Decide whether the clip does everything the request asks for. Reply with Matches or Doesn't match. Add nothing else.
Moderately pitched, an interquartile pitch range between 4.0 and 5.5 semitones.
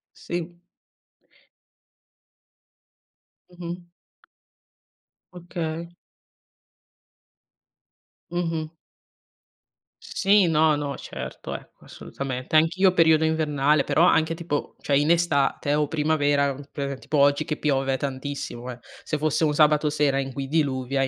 Doesn't match